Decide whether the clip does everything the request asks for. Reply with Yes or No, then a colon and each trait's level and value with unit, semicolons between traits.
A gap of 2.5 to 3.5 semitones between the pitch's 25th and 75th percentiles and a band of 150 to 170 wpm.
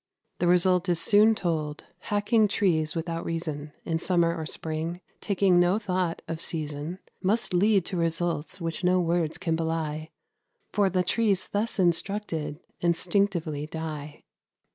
No: average, 2.8 semitones; average, 140 wpm